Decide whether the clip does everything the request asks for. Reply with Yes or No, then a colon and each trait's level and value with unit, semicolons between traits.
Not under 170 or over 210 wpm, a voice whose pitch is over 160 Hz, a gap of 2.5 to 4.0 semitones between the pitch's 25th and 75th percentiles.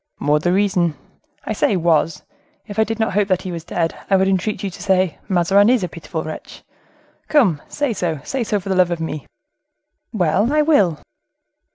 Yes: average, 190 wpm; medium, 185 Hz; average, 3.7 semitones